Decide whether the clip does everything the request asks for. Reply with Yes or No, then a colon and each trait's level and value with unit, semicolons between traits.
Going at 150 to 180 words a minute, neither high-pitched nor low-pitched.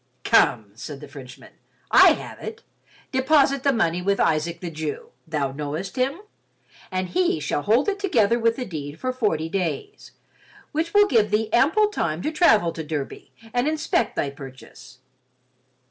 No: average, 155 wpm; high, 200 Hz